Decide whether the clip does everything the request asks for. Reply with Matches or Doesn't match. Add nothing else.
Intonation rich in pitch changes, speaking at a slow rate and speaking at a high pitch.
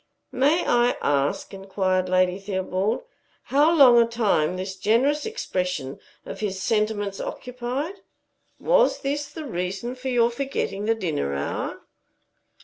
Matches